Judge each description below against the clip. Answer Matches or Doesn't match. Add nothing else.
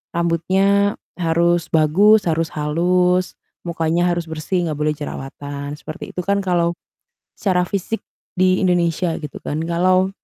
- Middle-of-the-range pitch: Matches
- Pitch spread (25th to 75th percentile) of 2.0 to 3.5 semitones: Matches